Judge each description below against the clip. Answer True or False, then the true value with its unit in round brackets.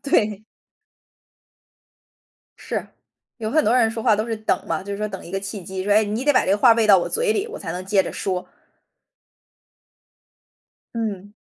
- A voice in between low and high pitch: False (210 Hz)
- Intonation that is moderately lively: True (3.0 semitones)